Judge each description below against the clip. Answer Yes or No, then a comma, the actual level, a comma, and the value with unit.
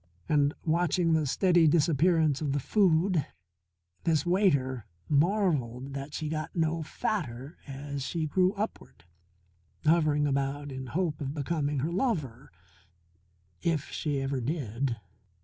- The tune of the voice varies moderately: Yes, average, 3.5 semitones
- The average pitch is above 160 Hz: No, medium, 150 Hz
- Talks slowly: Yes, slow, 125 wpm